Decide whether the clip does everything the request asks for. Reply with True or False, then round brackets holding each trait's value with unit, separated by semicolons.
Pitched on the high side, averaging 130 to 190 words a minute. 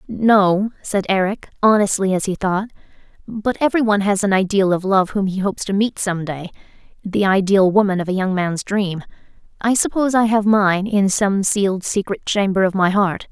True (200 Hz; 185 wpm)